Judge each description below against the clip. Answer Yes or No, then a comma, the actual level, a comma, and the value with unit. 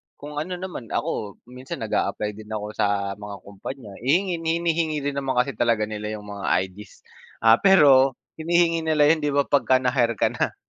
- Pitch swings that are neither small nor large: No, wide, 6.7 semitones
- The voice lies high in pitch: No, low, 130 Hz